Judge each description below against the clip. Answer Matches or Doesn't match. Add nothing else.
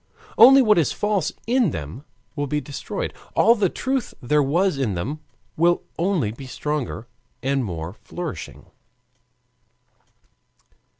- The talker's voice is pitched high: Doesn't match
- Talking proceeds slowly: Matches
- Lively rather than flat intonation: Matches